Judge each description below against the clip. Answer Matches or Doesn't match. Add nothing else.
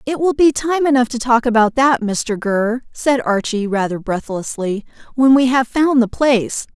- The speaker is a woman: Matches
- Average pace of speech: Matches